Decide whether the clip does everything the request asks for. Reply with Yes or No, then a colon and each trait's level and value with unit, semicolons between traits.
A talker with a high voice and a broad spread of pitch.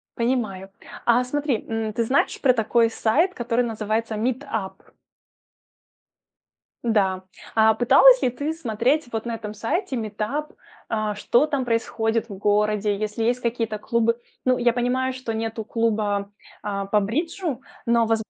No: high, 230 Hz; average, 2.7 semitones